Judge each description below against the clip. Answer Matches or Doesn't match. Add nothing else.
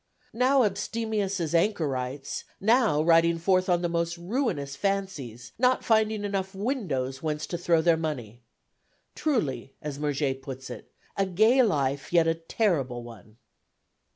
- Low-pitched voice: Doesn't match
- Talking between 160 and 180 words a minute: Doesn't match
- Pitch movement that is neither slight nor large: Doesn't match